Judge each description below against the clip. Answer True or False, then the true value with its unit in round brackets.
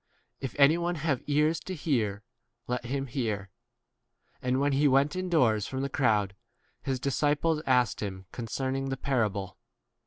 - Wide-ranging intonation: False (4.4 semitones)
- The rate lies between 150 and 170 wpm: True (160 wpm)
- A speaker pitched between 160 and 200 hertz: False (135 Hz)